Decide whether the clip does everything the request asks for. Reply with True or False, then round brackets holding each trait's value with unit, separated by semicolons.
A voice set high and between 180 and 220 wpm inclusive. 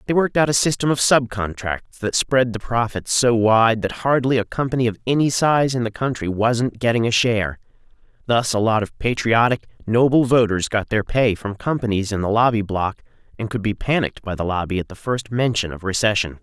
False (115 Hz; 205 wpm)